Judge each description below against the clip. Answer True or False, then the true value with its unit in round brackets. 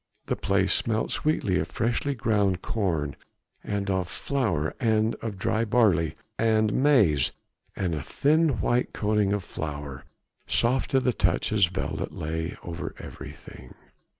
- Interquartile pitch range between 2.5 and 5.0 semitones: False (5.4 semitones)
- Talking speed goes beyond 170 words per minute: False (135 wpm)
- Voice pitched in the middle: False (105 Hz)